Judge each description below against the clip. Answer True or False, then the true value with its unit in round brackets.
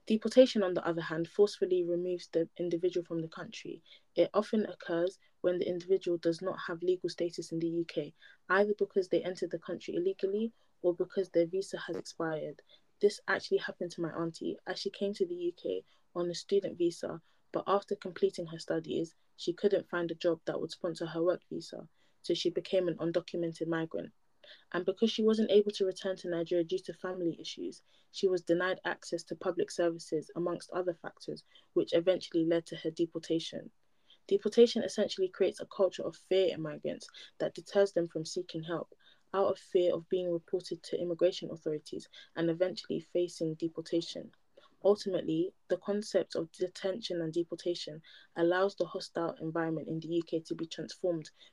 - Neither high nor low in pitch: True (180 Hz)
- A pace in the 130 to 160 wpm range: False (175 wpm)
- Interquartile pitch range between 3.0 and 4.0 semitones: False (2.5 semitones)